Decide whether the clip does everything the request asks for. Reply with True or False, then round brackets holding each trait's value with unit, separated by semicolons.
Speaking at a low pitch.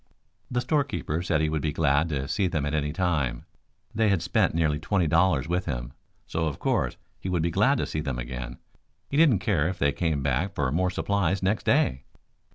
True (80 Hz)